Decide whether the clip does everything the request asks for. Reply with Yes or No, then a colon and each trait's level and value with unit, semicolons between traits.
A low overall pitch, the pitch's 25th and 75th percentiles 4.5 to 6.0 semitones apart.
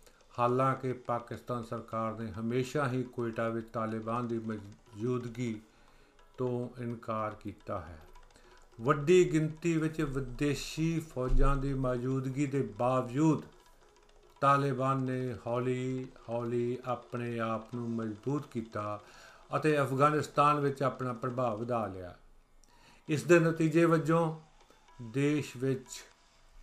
No: low, 125 Hz; average, 3.3 semitones